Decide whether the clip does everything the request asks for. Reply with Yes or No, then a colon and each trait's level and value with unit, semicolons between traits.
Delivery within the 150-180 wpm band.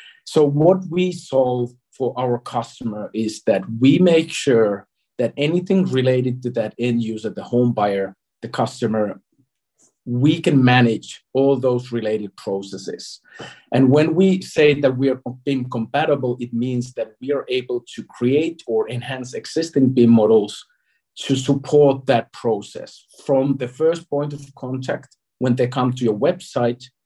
Yes: average, 155 wpm